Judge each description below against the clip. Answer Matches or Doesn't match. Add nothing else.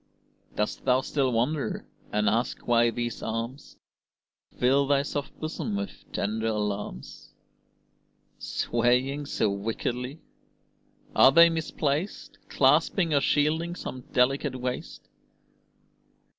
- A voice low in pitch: Matches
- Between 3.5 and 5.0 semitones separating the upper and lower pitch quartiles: Matches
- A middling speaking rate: Doesn't match